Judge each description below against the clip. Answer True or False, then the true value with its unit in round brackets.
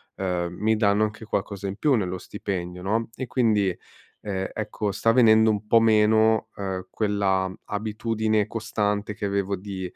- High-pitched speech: False (105 Hz)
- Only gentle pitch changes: True (2.2 semitones)